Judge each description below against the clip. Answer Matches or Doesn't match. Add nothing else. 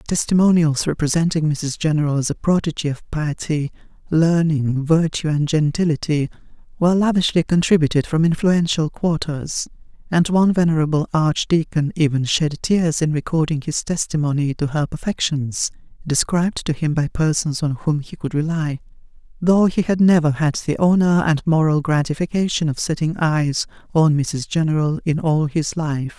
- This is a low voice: Doesn't match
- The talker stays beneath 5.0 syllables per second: Matches